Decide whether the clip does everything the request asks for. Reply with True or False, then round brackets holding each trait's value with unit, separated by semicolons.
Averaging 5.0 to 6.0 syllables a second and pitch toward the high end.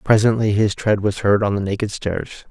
False (5.1 syllables/s; 105 Hz)